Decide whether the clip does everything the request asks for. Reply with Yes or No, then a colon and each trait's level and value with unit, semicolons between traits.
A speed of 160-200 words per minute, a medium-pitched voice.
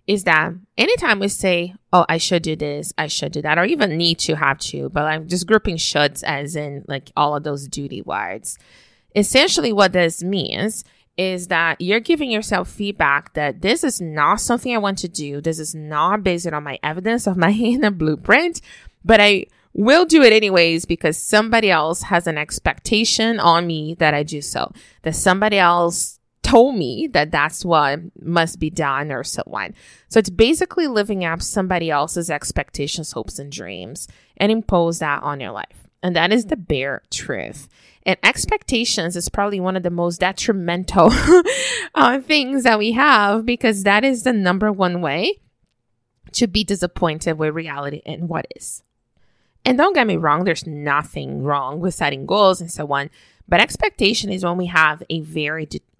Yes: average, 180 wpm; medium, 175 Hz